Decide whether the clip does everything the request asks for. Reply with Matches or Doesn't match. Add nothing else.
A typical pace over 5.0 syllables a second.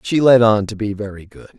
Matches